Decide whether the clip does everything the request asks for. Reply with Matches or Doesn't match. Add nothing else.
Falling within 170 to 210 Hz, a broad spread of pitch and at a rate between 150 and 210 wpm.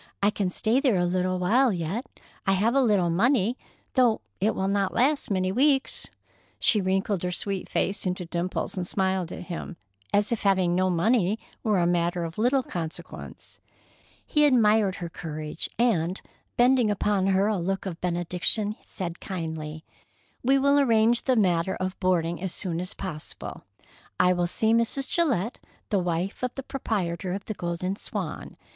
Doesn't match